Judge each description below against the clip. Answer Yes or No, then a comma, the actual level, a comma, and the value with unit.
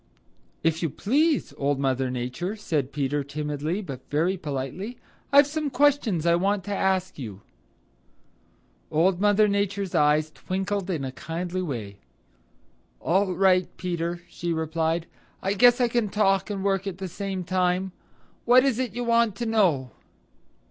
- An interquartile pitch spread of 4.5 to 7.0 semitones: Yes, average, 4.9 semitones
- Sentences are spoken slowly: No, average, 150 wpm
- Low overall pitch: No, medium, 185 Hz